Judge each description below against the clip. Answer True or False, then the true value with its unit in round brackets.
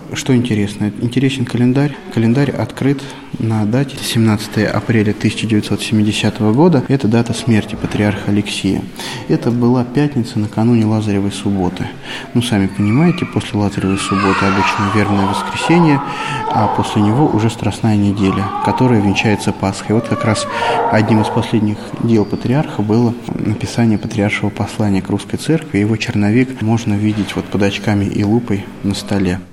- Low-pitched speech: True (110 Hz)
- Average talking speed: True (135 wpm)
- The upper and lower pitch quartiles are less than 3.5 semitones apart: True (2.9 semitones)